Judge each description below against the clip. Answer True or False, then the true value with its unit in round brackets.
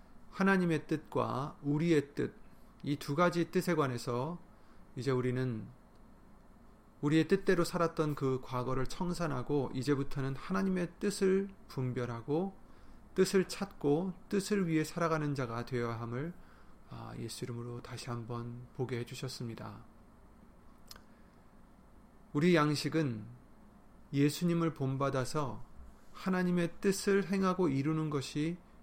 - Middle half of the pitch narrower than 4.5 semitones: False (5.5 semitones)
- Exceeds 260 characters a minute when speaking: False (250 characters per minute)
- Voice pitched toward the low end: False (150 Hz)